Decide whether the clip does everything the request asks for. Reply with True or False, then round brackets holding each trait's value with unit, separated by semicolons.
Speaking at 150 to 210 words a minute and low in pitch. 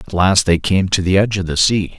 False (300 wpm; 95 Hz)